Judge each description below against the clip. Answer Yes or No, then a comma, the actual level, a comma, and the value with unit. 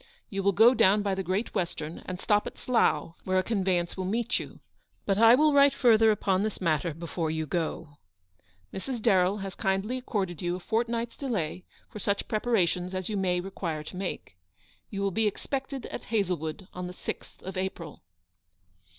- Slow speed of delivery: No, average, 185 wpm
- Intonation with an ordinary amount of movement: Yes, average, 3.6 semitones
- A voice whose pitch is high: Yes, high, 195 Hz